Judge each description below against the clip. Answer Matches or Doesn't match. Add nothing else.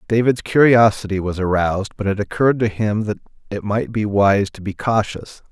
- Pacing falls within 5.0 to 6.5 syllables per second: Matches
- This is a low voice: Matches